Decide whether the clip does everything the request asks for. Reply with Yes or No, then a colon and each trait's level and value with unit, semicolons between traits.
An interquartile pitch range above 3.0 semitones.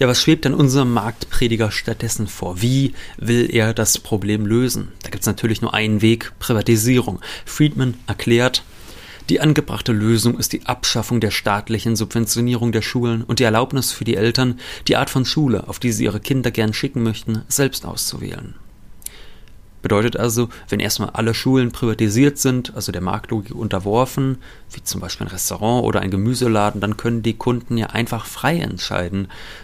No: narrow, 2.6 semitones